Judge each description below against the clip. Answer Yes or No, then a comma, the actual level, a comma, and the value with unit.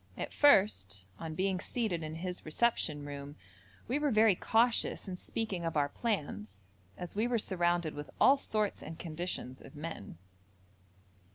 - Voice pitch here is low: No, medium, 175 Hz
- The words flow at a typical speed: Yes, average, 155 wpm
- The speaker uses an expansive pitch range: Yes, wide, 6.3 semitones